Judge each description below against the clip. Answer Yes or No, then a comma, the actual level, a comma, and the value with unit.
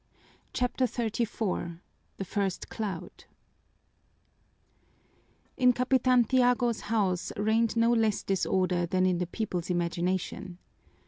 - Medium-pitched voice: No, high, 210 Hz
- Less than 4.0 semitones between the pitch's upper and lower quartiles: No, average, 4.6 semitones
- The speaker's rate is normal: No, slow, 100 wpm